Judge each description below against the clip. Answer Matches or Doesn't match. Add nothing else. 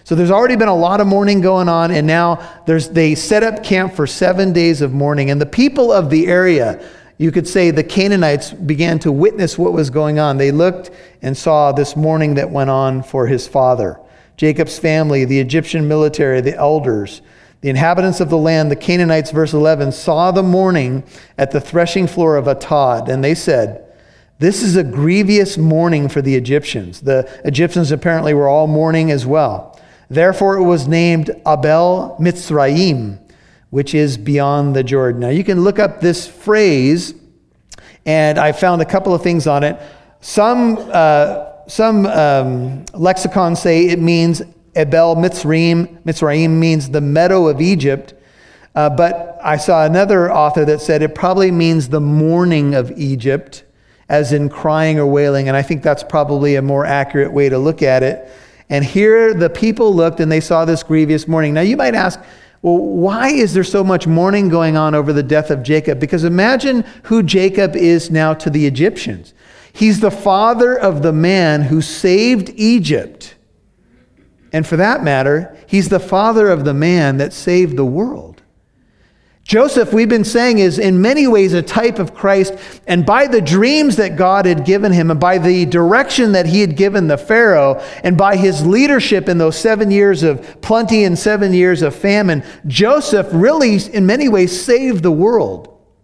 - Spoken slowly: Doesn't match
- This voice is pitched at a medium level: Matches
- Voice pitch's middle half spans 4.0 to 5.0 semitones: Matches